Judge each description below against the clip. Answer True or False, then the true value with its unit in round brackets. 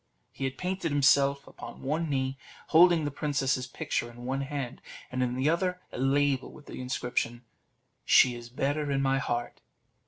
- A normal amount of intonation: False (2.3 semitones)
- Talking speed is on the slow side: False (175 wpm)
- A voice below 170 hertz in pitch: True (135 Hz)